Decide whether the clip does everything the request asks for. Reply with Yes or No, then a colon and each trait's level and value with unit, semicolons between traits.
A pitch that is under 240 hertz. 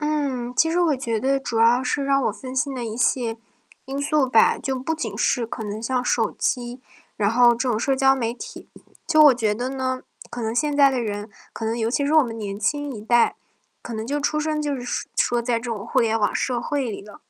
No: very high, 250 Hz